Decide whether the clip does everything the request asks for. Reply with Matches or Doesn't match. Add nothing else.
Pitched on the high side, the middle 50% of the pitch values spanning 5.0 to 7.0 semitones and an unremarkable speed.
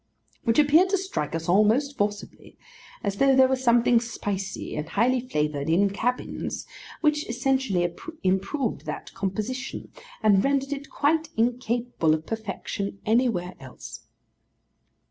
Doesn't match